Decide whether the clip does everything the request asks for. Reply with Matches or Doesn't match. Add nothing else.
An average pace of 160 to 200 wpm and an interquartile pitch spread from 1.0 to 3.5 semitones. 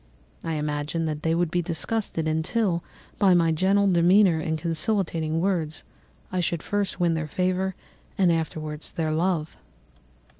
Doesn't match